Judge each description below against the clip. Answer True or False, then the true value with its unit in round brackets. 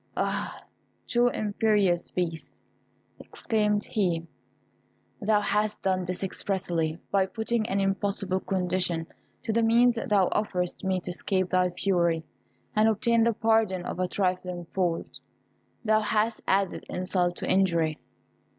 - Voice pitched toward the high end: True (195 Hz)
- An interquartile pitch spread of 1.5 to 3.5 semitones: True (3.0 semitones)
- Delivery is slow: True (130 wpm)